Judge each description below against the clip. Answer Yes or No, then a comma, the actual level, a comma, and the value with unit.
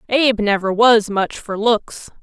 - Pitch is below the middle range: No, high, 220 Hz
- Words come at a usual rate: Yes, average, 160 wpm